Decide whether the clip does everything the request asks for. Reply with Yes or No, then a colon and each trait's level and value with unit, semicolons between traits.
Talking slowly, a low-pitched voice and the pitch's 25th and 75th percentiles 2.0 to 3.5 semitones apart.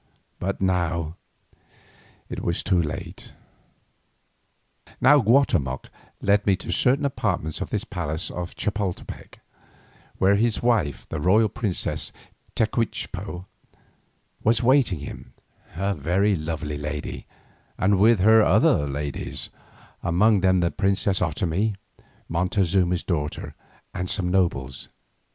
No: slow, 110 wpm; very low, 95 Hz; average, 4.0 semitones